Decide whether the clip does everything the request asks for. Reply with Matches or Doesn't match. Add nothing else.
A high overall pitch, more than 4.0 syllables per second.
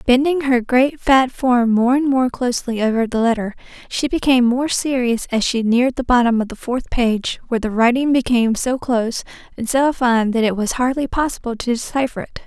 Matches